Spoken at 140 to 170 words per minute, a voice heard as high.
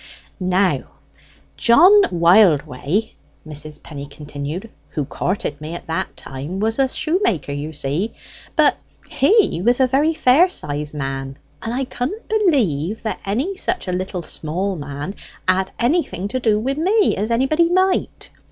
Yes: average, 145 wpm; high, 195 Hz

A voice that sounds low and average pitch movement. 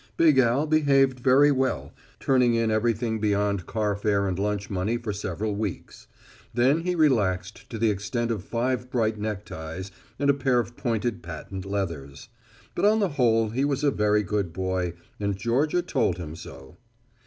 Yes: low, 110 Hz; average, 4.5 semitones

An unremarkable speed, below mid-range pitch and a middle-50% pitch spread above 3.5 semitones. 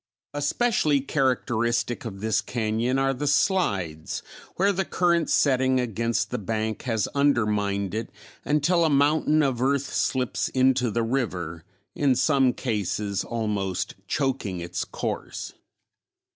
No: slow, 125 wpm; low, 125 Hz; average, 4.8 semitones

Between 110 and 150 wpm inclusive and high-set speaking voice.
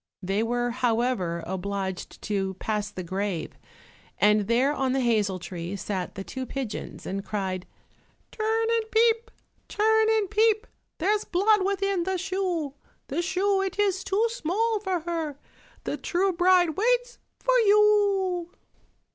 Yes: average, 140 wpm; very high, 345 Hz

